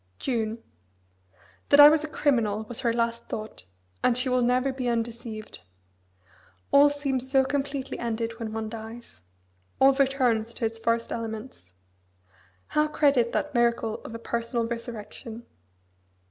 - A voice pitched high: Yes, high, 235 Hz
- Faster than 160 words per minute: No, average, 140 wpm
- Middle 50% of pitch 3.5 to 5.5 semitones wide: No, average, 2.8 semitones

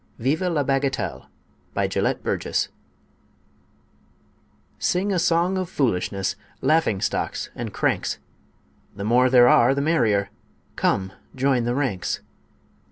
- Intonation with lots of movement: Yes, wide, 6.0 semitones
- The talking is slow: Yes, slow, 115 wpm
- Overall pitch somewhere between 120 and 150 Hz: Yes, low, 135 Hz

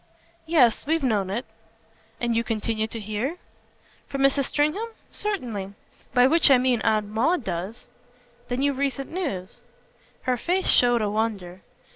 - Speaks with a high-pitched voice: Yes, high, 245 Hz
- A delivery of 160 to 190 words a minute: No, average, 145 wpm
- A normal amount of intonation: Yes, average, 4.6 semitones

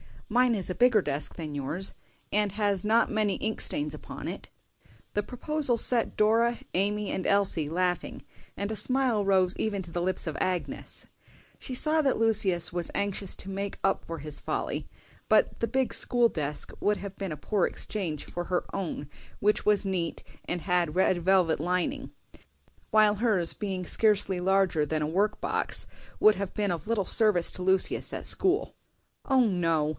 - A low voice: No, high, 195 Hz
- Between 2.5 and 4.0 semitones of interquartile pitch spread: Yes, average, 3.5 semitones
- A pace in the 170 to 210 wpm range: Yes, average, 175 wpm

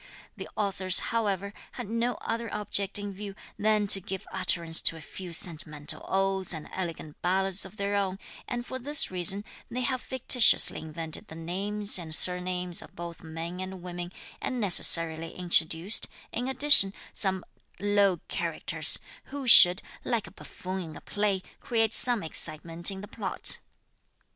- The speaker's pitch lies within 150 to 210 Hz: Yes, high, 190 Hz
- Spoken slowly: No, average, 155 wpm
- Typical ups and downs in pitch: Yes, average, 3.3 semitones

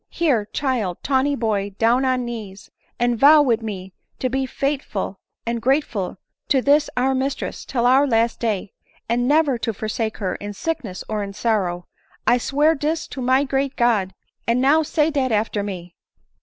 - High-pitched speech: Yes, high, 240 Hz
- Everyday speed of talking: Yes, average, 175 wpm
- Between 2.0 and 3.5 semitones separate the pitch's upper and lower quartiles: No, average, 4.5 semitones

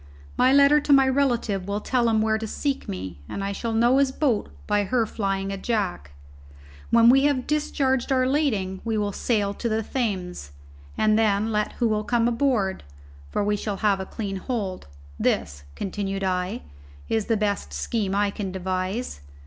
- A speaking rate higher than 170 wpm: Yes, average, 180 wpm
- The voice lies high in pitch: Yes, high, 215 Hz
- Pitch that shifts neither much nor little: Yes, average, 3.9 semitones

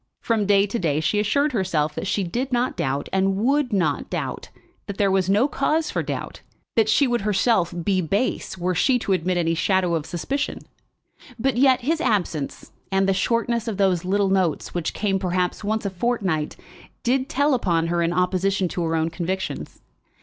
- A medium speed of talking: Yes, average, 190 wpm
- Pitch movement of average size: Yes, average, 5.0 semitones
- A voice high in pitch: Yes, high, 195 Hz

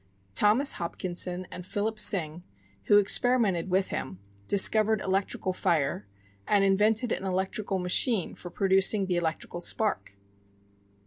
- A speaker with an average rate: No, slow, 120 wpm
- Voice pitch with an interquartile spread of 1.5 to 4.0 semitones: Yes, average, 2.8 semitones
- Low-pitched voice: No, high, 190 Hz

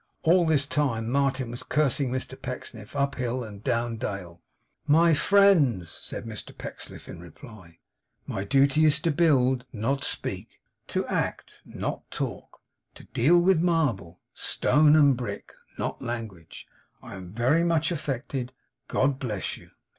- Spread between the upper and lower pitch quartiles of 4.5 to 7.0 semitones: Yes, average, 5.0 semitones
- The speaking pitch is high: No, low, 130 Hz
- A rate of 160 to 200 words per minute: No, average, 145 wpm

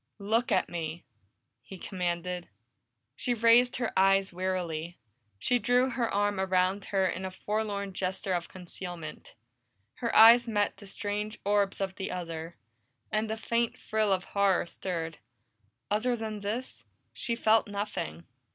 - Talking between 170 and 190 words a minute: No, average, 140 wpm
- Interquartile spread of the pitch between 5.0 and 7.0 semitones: No, average, 3.2 semitones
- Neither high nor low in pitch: No, high, 200 Hz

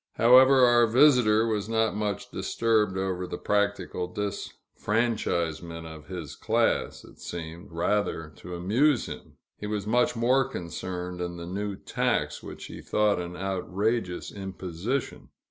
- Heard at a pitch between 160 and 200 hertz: No, low, 100 Hz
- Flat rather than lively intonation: No, average, 4.3 semitones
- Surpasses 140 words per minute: No, slow, 135 wpm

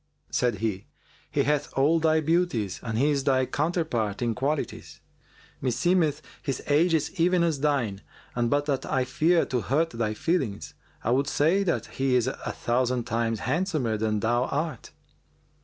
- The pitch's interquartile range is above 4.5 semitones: Yes, average, 5.0 semitones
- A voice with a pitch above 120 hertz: Yes, low, 135 Hz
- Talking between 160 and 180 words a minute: Yes, average, 165 wpm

